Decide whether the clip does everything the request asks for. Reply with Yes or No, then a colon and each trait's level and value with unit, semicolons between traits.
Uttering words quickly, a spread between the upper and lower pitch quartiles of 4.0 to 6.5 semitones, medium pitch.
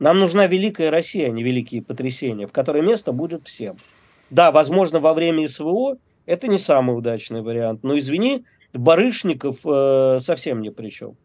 Yes: fast, 165 wpm; wide, 5.6 semitones; medium, 145 Hz